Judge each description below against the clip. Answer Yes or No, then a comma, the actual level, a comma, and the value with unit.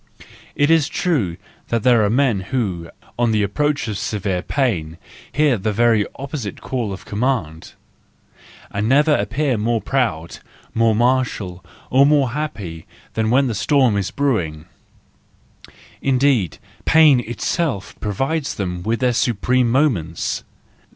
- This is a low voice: Yes, low, 115 Hz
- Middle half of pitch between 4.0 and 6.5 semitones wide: Yes, average, 5.3 semitones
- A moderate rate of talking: No, slow, 130 wpm